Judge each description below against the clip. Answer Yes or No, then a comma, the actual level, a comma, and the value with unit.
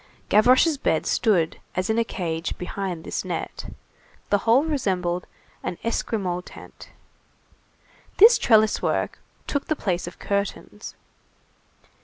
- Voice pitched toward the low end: No, high, 200 Hz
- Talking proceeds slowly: Yes, slow, 120 wpm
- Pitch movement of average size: Yes, average, 4.5 semitones